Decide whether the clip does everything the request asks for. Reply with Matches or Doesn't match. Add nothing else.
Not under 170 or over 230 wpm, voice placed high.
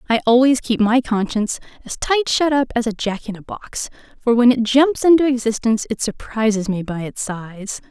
Matches